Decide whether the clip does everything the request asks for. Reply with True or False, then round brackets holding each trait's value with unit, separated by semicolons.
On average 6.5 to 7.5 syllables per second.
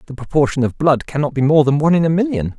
True (7.0 syllables/s)